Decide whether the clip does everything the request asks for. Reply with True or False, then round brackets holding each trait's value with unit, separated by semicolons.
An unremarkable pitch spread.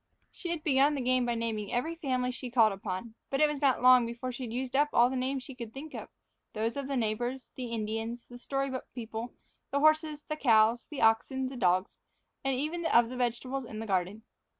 True (3.1 semitones)